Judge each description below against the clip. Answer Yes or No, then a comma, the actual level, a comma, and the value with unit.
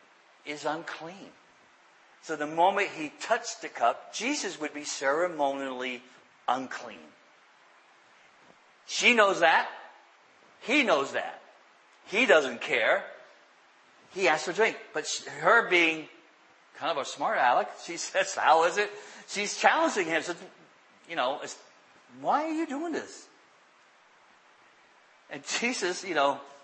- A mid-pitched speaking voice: Yes, medium, 165 Hz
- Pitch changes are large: Yes, wide, 5.9 semitones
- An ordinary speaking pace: No, slow, 125 wpm